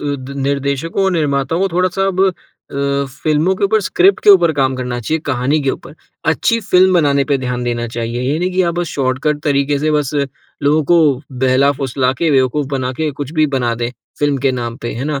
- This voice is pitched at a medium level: Yes, medium, 145 Hz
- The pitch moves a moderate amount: Yes, average, 4.1 semitones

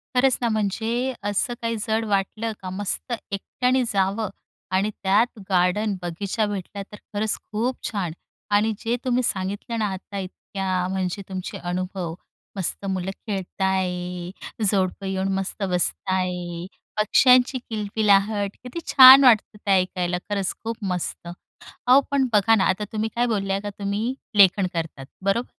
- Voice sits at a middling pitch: No, high, 200 Hz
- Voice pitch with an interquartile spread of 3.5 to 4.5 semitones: No, average, 2.9 semitones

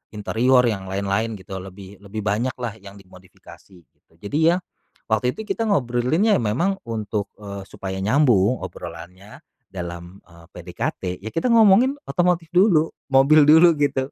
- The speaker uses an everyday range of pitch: No, wide, 7.7 semitones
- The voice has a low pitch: Yes, low, 110 Hz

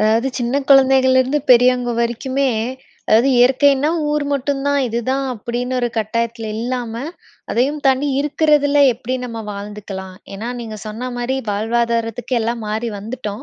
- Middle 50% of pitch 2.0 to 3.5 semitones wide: Yes, average, 2.9 semitones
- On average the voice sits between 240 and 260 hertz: Yes, high, 245 Hz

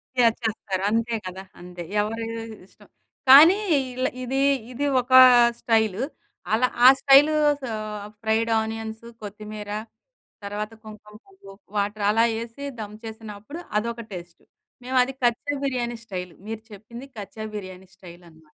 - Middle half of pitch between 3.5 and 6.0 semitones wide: No, average, 2.8 semitones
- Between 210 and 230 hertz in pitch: Yes, high, 220 Hz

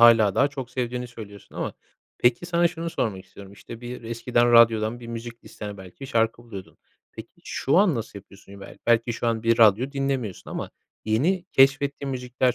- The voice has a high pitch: No, low, 120 Hz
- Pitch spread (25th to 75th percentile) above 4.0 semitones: No, average, 3.2 semitones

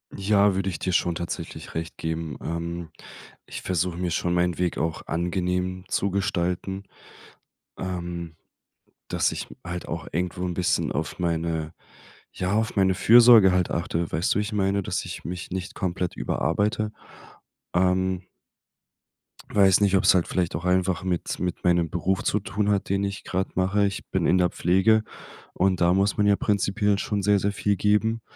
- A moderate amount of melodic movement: No, narrow, 2.3 semitones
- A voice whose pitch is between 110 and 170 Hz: No, very low, 90 Hz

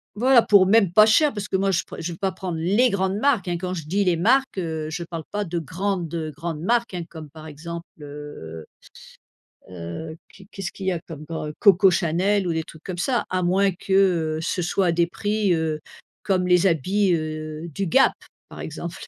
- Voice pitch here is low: No, medium, 175 Hz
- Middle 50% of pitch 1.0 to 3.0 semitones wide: No, average, 3.6 semitones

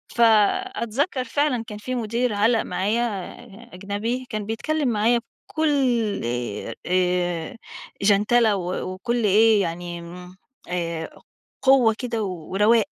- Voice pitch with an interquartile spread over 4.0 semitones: Yes, average, 4.7 semitones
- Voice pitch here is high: Yes, high, 215 Hz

